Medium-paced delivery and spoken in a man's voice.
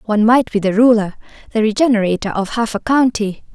No: average, 185 wpm; female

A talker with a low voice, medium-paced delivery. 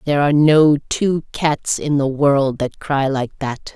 No: medium, 145 Hz; average, 190 wpm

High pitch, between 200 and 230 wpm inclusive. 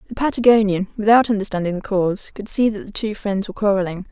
Yes: high, 205 Hz; fast, 205 wpm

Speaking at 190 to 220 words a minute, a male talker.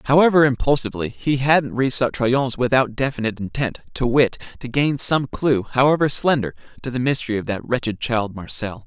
No: average, 170 wpm; male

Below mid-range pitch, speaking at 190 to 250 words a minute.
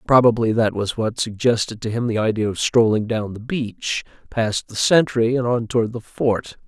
Yes: low, 115 Hz; average, 200 wpm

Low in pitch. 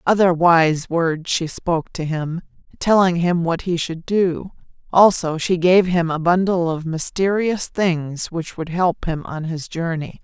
No: medium, 170 Hz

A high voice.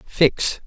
No: medium, 140 Hz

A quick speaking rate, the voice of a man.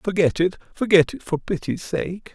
No: average, 180 wpm; male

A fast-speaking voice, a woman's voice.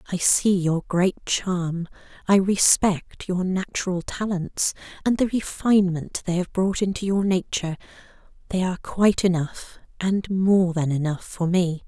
No: average, 140 wpm; female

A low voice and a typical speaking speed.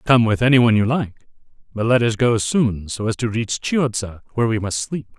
No: low, 115 Hz; fast, 220 wpm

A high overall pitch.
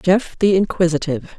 No: medium, 175 Hz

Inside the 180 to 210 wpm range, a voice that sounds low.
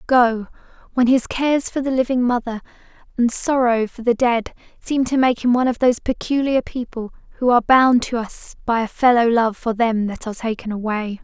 No: average, 200 wpm; high, 240 Hz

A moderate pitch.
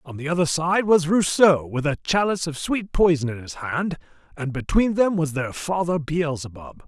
Yes: medium, 160 Hz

